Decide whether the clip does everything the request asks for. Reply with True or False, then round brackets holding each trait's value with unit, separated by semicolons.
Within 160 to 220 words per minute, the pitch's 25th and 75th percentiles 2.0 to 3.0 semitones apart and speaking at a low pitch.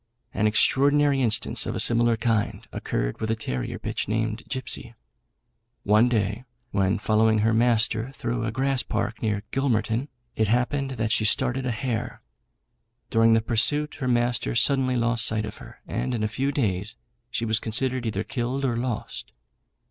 True (165 wpm; 2.7 semitones; 115 Hz)